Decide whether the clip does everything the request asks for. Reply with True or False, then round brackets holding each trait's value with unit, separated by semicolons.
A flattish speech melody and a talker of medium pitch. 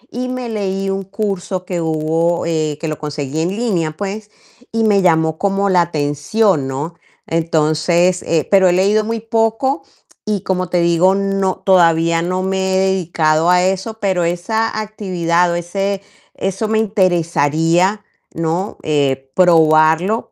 False (3.4 semitones; 180 Hz)